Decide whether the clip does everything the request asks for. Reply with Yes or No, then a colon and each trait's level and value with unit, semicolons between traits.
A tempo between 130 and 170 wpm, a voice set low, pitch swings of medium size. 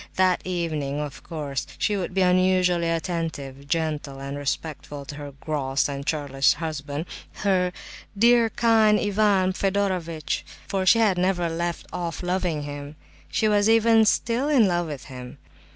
No: average, 150 wpm; medium, 170 Hz; average, 4.9 semitones